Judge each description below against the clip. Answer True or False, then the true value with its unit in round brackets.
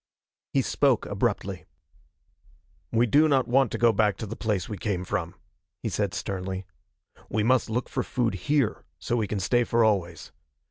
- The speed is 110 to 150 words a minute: False (175 wpm)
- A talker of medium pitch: False (110 Hz)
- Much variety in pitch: False (3.8 semitones)